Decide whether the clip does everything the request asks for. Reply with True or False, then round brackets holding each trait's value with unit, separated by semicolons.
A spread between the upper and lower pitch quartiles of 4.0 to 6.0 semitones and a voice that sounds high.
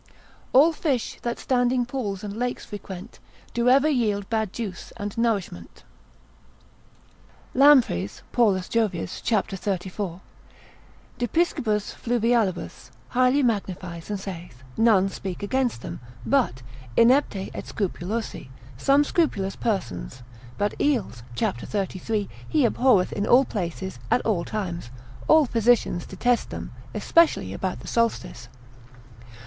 True (4.5 semitones; 215 Hz)